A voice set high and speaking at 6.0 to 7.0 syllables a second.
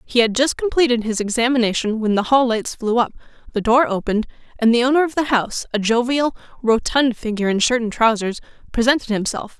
Yes: high, 235 Hz; 6.1 syllables/s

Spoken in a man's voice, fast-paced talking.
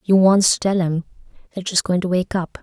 No: female; fast, 250 wpm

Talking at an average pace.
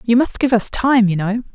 No: fast, 270 wpm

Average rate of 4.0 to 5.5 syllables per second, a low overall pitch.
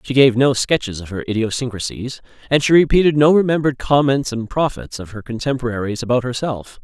No: 5.9 syllables/s; low, 125 Hz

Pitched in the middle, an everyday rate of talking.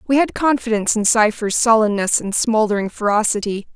No: high, 220 Hz; average, 145 wpm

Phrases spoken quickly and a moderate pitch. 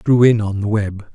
No: fast, 315 wpm; low, 105 Hz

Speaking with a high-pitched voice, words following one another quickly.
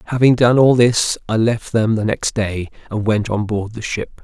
No: low, 110 Hz; fast, 225 wpm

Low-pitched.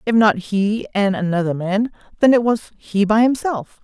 No: high, 210 Hz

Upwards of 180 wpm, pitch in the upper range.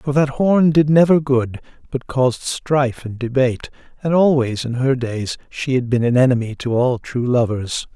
No: average, 190 wpm; low, 130 Hz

